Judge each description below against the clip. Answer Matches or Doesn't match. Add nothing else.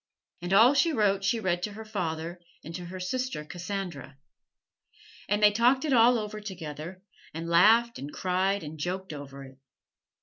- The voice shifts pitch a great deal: Doesn't match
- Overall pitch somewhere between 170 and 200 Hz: Matches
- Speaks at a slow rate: Doesn't match